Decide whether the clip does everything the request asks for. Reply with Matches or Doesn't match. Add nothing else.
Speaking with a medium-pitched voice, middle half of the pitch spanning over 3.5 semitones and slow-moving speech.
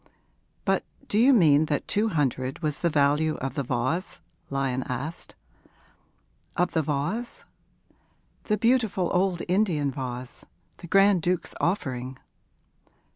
Matches